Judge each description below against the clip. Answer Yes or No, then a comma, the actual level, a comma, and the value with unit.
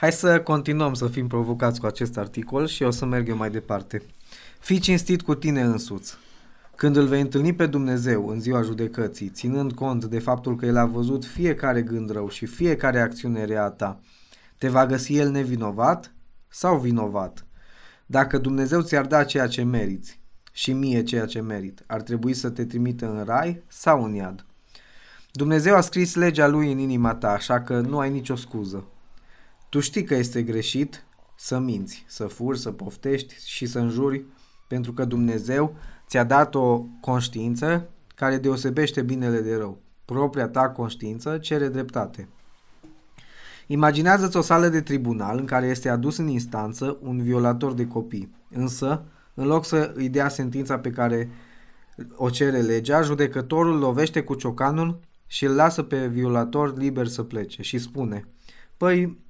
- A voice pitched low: Yes, low, 130 Hz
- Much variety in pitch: No, average, 3.5 semitones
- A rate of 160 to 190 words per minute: Yes, average, 165 wpm